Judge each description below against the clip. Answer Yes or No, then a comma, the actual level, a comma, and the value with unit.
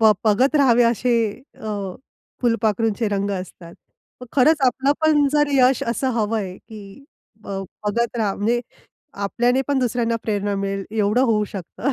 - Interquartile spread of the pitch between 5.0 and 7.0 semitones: No, average, 3.7 semitones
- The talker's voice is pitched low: No, high, 225 Hz